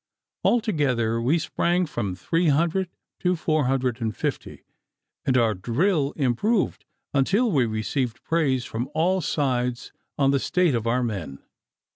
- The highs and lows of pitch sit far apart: Yes, wide, 6.0 semitones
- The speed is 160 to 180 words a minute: No, average, 140 wpm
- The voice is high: No, low, 135 Hz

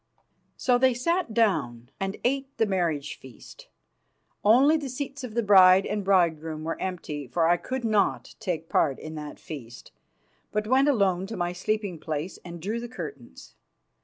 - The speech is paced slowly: No, average, 165 wpm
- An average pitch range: No, wide, 6.5 semitones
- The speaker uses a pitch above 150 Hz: Yes, high, 190 Hz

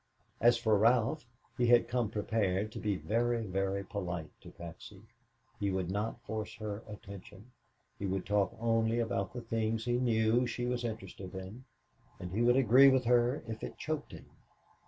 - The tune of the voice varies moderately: Yes, average, 3.3 semitones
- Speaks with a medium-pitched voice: No, low, 110 Hz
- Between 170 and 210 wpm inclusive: Yes, average, 175 wpm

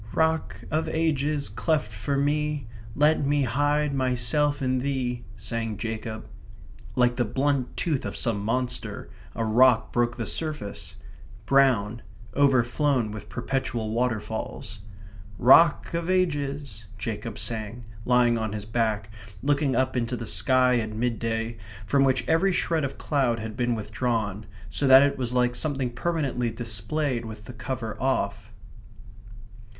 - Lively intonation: No, average, 4.1 semitones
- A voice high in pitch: No, low, 125 Hz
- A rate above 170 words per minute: No, average, 145 wpm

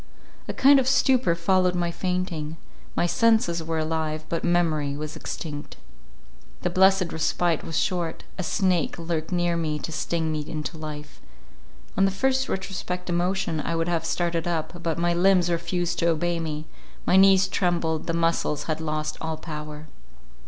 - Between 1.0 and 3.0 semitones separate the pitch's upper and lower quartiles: Yes, narrow, 2.4 semitones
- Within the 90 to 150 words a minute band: No, average, 160 wpm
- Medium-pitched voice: Yes, medium, 170 Hz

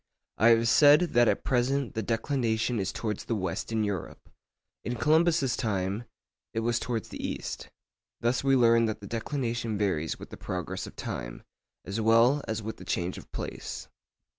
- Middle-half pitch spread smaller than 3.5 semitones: Yes, average, 2.8 semitones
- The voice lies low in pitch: Yes, low, 115 Hz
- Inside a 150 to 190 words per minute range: Yes, average, 170 wpm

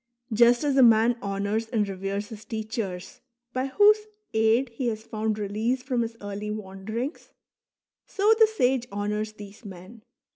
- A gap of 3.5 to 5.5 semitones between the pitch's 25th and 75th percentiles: No, average, 3.0 semitones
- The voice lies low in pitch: No, high, 220 Hz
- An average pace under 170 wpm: Yes, average, 150 wpm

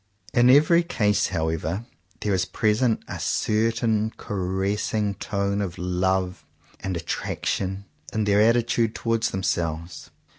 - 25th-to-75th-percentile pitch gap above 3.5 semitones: No, average, 3.2 semitones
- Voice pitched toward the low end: Yes, low, 100 Hz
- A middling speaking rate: No, slow, 125 wpm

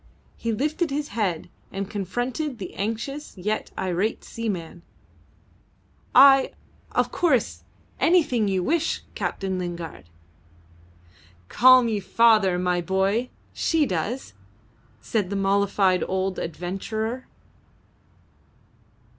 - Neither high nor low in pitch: No, high, 210 Hz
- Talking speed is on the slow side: Yes, slow, 95 wpm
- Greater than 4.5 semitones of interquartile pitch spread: Yes, average, 5.2 semitones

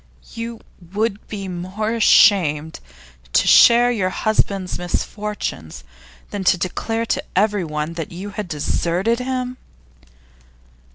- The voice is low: No, high, 200 Hz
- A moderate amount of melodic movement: Yes, average, 4.4 semitones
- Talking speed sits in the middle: No, slow, 110 wpm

